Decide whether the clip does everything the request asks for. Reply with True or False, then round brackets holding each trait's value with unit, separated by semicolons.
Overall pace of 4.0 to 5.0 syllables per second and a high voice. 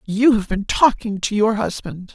True (4.5 syllables/s; 210 Hz)